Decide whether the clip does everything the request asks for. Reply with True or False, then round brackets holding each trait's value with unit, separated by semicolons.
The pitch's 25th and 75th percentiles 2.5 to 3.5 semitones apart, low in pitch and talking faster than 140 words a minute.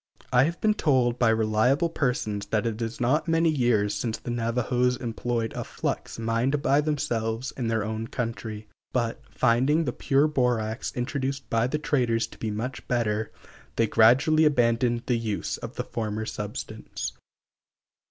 True (3.0 semitones; 120 Hz; 160 wpm)